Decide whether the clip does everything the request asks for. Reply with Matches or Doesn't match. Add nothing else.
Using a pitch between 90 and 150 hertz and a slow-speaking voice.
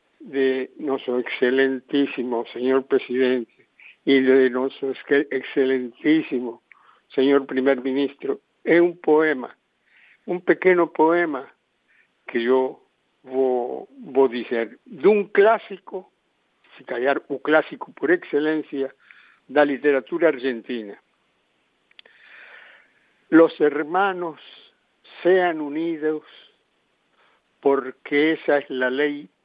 Matches